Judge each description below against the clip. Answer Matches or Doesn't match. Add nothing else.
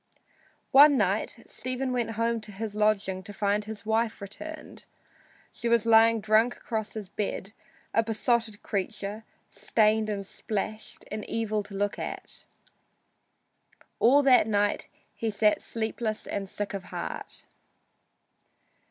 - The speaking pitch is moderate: Doesn't match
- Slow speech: Matches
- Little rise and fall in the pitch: Matches